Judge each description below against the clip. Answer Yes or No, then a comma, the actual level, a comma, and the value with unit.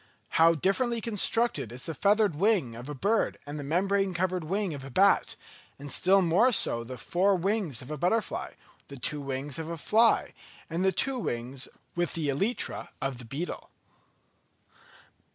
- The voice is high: No, medium, 170 Hz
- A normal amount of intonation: No, wide, 6.2 semitones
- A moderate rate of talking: Yes, average, 170 wpm